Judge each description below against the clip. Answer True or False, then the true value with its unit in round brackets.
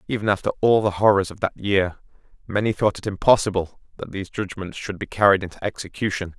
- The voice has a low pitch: True (100 Hz)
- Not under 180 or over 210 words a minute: True (190 wpm)